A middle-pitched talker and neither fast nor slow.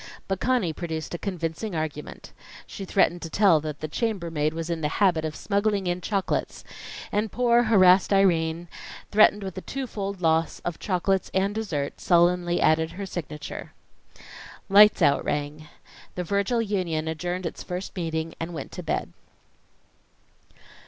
Yes: medium, 180 Hz; average, 150 wpm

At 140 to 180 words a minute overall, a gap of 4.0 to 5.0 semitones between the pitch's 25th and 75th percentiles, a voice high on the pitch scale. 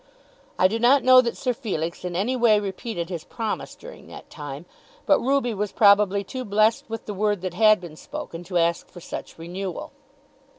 No: average, 195 wpm; average, 4.6 semitones; high, 205 Hz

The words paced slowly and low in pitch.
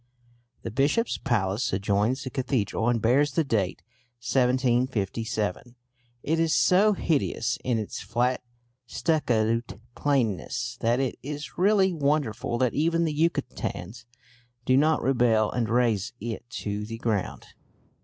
Yes: slow, 125 wpm; low, 125 Hz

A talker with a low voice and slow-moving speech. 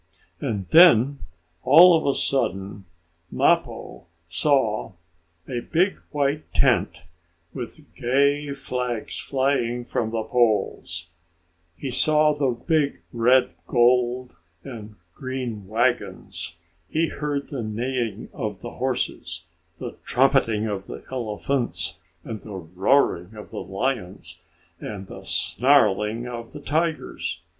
Yes: low, 125 Hz; slow, 110 wpm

